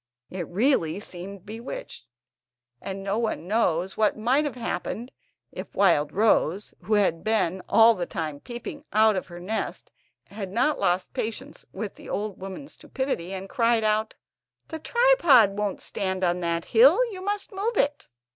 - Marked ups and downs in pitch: No, average, 4.8 semitones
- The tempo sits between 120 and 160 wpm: Yes, average, 155 wpm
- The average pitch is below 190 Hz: No, high, 210 Hz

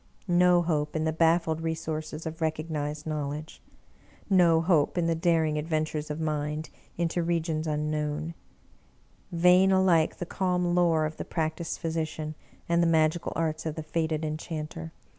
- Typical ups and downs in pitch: No, narrow, 1.5 semitones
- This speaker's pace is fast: No, average, 150 wpm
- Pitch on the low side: No, medium, 160 Hz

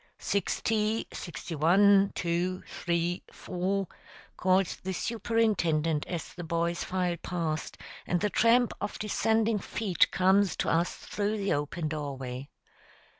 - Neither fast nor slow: No, slow, 125 wpm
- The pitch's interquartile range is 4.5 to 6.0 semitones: No, average, 3.4 semitones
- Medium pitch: Yes, medium, 180 Hz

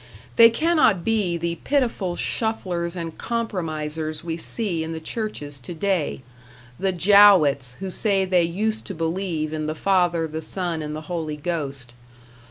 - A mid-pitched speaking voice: Yes, medium, 170 Hz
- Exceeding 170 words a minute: No, average, 150 wpm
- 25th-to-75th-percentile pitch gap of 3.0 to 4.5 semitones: Yes, average, 3.9 semitones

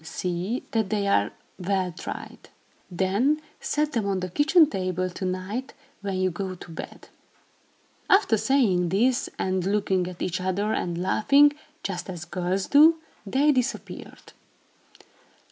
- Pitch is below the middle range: No, high, 195 Hz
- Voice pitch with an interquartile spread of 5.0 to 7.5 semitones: Yes, wide, 5.6 semitones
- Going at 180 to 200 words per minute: No, average, 140 wpm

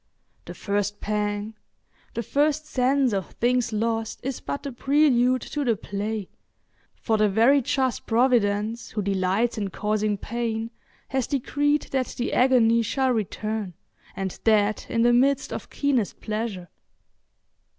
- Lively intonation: No, average, 3.6 semitones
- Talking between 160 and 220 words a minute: No, slow, 135 wpm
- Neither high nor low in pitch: No, high, 230 Hz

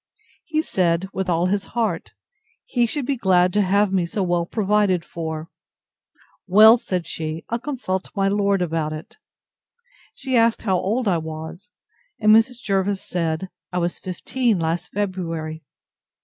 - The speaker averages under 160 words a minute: Yes, average, 150 wpm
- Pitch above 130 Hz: Yes, high, 190 Hz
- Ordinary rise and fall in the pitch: Yes, average, 3.9 semitones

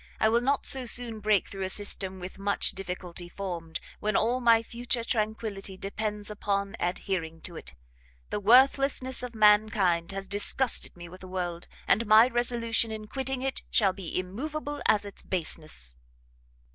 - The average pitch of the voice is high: Yes, high, 210 Hz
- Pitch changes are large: No, average, 3.9 semitones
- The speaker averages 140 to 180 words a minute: Yes, average, 160 wpm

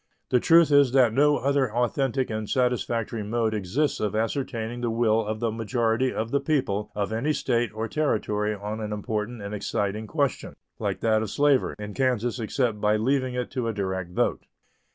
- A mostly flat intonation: No, average, 3.3 semitones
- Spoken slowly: No, average, 185 wpm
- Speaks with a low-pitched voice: Yes, low, 115 Hz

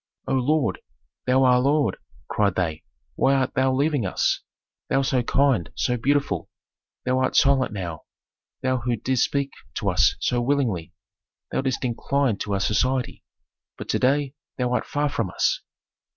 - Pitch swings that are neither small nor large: Yes, average, 3.0 semitones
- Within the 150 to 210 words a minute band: Yes, average, 160 wpm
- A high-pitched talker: No, low, 130 Hz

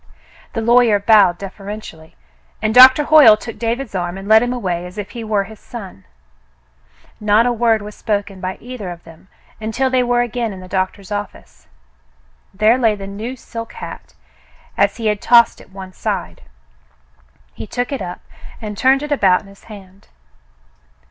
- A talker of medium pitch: No, high, 215 Hz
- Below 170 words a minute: No, average, 175 wpm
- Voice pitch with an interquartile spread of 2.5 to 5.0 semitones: Yes, average, 3.5 semitones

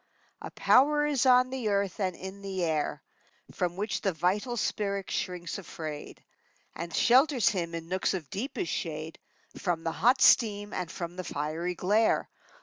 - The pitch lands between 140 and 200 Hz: Yes, high, 190 Hz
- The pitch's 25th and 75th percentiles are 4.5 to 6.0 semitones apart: Yes, average, 4.8 semitones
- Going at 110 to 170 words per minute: Yes, average, 160 wpm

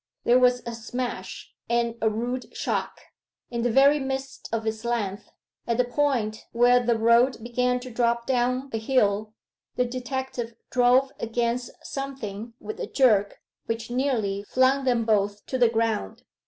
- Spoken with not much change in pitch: Yes, narrow, 2.2 semitones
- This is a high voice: Yes, high, 240 Hz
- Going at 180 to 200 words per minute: No, average, 155 wpm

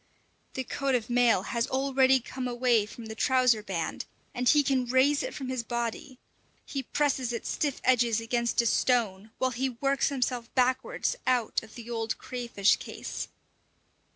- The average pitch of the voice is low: No, high, 245 Hz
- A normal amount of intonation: No, narrow, 2.1 semitones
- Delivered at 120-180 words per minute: Yes, average, 165 wpm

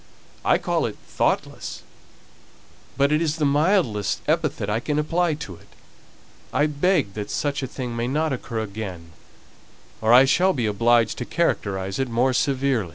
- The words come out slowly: No, average, 160 wpm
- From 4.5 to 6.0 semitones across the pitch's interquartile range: Yes, wide, 5.4 semitones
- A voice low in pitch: Yes, low, 130 Hz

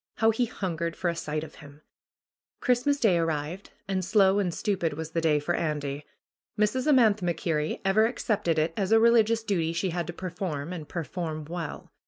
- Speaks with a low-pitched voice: No, medium, 175 Hz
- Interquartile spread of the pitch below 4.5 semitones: No, average, 4.8 semitones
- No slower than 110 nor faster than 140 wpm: No, average, 185 wpm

